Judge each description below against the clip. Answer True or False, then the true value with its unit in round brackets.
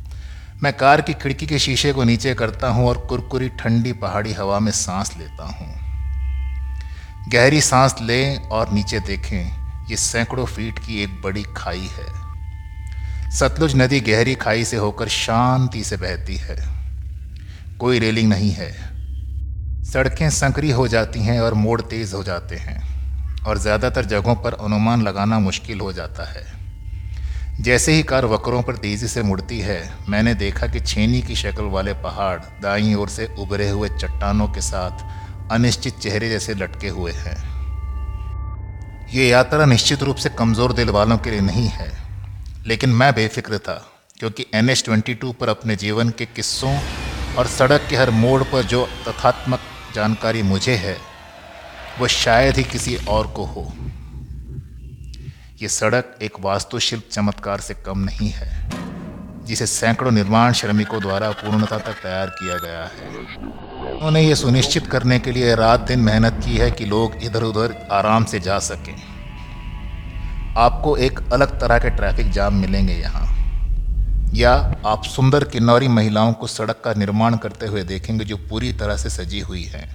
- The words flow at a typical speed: True (160 wpm)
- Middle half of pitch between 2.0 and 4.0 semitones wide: False (4.7 semitones)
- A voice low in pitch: True (105 Hz)